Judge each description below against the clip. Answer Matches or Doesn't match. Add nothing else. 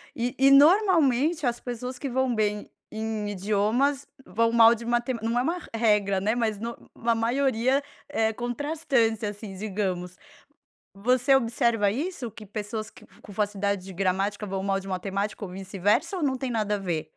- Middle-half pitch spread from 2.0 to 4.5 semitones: Matches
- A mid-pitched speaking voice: Doesn't match